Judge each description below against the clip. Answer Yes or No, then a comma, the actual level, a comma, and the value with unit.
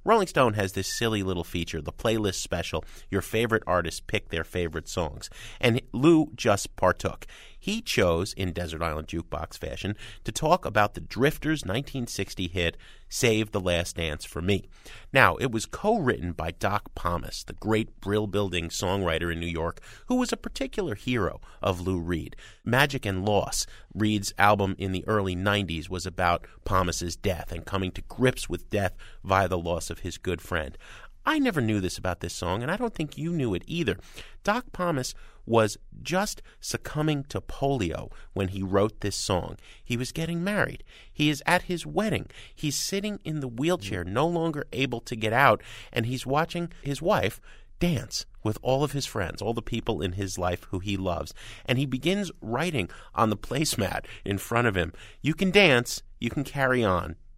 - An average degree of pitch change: No, wide, 6.9 semitones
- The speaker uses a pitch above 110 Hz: No, low, 105 Hz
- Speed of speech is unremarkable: Yes, average, 185 wpm